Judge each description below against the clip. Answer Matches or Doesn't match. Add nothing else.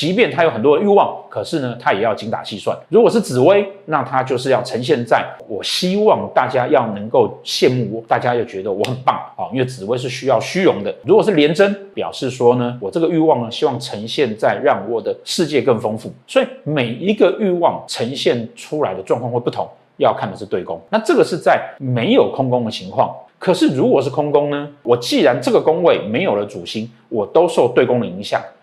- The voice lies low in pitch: Doesn't match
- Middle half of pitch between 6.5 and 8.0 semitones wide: Matches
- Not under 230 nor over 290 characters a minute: Doesn't match